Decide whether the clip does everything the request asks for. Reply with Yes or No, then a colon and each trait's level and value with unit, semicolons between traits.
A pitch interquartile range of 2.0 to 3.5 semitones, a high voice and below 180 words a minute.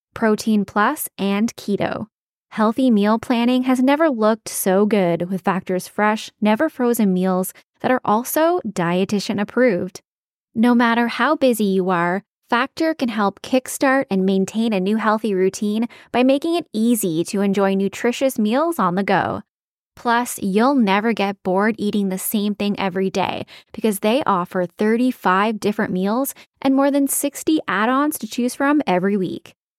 No: average, 4.3 semitones; high, 215 Hz; average, 155 wpm